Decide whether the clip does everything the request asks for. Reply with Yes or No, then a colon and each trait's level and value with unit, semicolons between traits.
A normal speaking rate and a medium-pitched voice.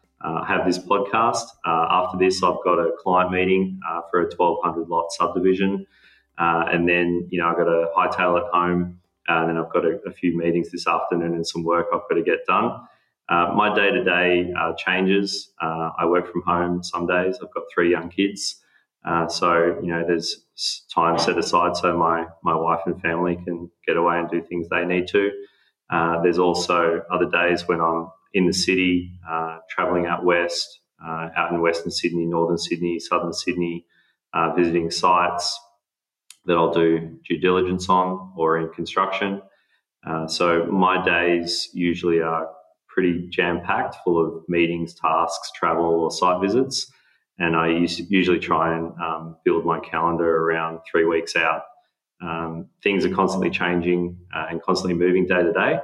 No: average, 180 wpm; very low, 85 Hz